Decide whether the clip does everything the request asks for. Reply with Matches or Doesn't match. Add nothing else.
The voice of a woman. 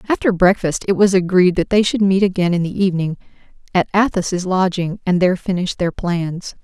Matches